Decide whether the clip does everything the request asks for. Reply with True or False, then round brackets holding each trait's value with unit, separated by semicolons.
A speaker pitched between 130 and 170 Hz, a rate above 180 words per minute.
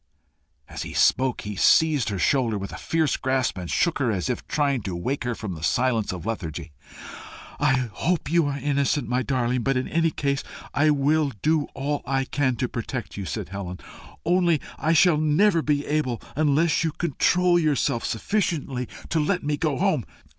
True (140 Hz; 190 wpm)